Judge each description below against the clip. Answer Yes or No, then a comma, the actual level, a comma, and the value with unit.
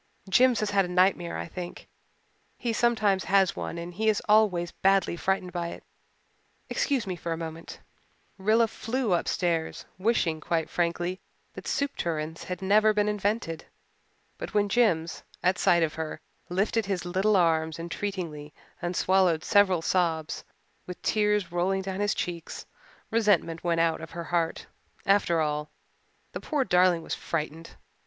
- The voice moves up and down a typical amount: Yes, average, 3.6 semitones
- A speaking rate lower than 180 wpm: Yes, average, 155 wpm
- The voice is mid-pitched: Yes, medium, 180 Hz